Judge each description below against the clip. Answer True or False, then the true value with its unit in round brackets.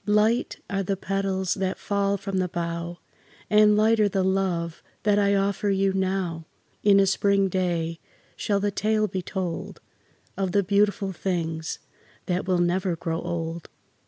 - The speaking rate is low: False (155 wpm)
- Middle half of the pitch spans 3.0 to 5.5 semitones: False (2.4 semitones)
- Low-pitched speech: False (190 Hz)